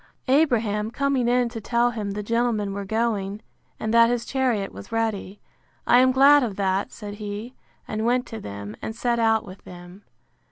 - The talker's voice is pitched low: No, high, 225 Hz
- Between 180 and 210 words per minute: Yes, average, 185 wpm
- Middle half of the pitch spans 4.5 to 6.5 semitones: No, average, 3.0 semitones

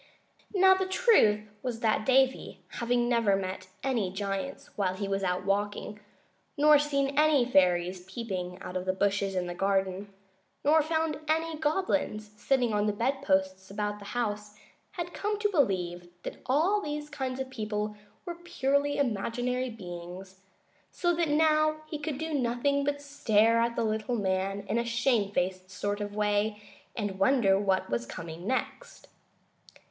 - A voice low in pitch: No, high, 225 Hz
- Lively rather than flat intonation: Yes, wide, 6.5 semitones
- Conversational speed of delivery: Yes, average, 155 wpm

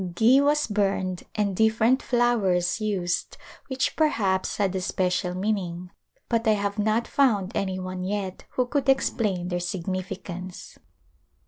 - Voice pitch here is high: Yes, high, 200 Hz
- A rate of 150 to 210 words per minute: No, average, 140 wpm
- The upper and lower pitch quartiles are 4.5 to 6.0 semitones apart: No, average, 3.7 semitones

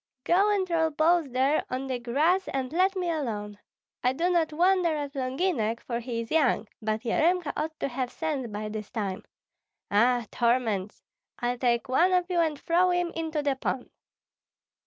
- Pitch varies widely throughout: Yes, wide, 5.9 semitones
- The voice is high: Yes, very high, 275 Hz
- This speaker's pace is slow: No, average, 180 wpm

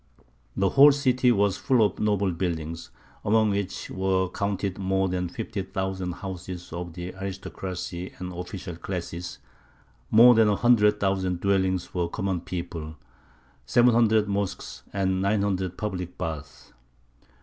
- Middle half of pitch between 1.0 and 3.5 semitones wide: Yes, narrow, 2.4 semitones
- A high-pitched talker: No, very low, 95 Hz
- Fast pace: No, average, 140 wpm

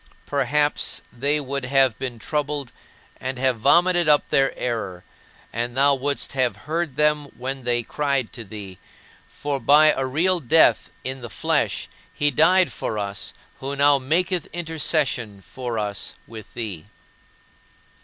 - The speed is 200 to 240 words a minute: No, average, 145 wpm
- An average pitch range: Yes, average, 3.8 semitones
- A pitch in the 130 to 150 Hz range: Yes, low, 135 Hz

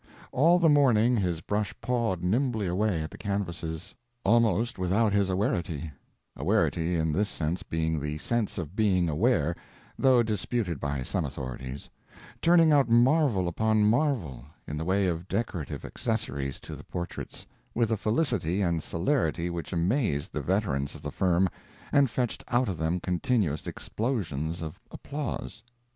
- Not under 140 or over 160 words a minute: Yes, average, 145 wpm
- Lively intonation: Yes, wide, 6.1 semitones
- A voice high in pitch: No, very low, 95 Hz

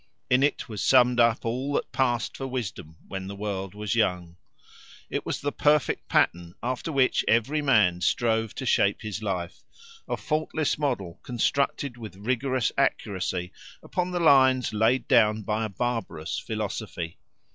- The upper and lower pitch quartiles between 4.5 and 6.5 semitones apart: Yes, average, 4.8 semitones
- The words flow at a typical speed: Yes, average, 155 wpm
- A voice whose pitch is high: No, low, 115 Hz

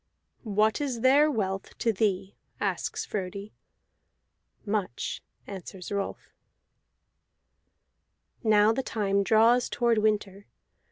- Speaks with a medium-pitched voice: No, high, 210 Hz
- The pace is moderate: No, slow, 95 wpm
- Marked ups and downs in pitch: No, narrow, 2.4 semitones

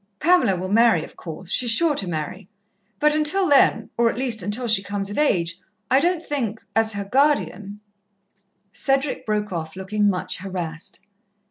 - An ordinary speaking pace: Yes, average, 170 wpm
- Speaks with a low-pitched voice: No, high, 210 Hz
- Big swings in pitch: Yes, wide, 6.0 semitones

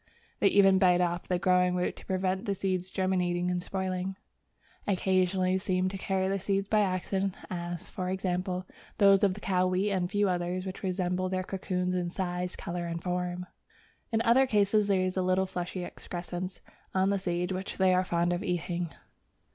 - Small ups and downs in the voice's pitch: Yes, narrow, 1.2 semitones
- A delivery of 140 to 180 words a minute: No, average, 190 wpm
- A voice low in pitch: No, medium, 185 Hz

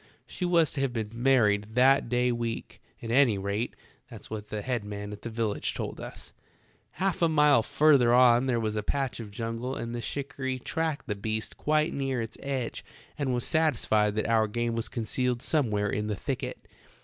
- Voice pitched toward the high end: No, low, 120 Hz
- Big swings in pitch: No, average, 3.8 semitones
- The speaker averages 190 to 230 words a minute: Yes, average, 195 wpm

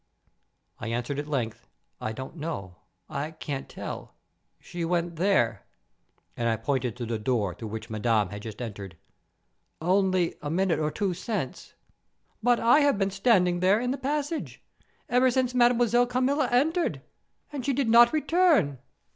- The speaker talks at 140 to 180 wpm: Yes, average, 150 wpm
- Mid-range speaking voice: Yes, medium, 175 Hz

